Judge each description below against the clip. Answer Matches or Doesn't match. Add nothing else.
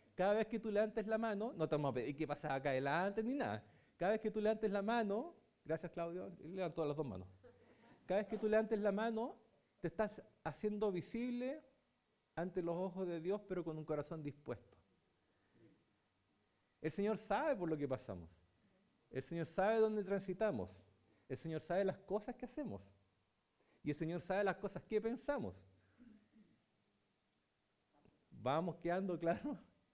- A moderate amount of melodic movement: Doesn't match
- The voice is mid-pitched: Matches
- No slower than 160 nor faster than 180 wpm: Matches